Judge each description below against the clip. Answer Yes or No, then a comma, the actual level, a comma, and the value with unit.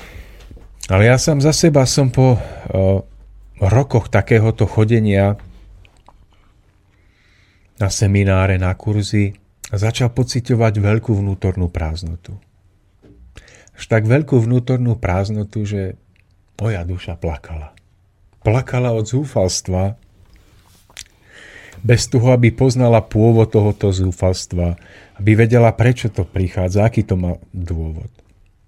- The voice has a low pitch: Yes, low, 100 Hz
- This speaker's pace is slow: Yes, slow, 100 wpm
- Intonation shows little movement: No, average, 3.3 semitones